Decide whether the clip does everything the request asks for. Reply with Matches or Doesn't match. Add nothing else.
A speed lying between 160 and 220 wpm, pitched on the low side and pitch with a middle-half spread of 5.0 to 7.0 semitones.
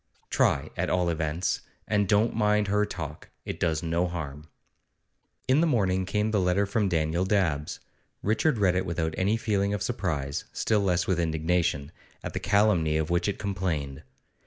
Doesn't match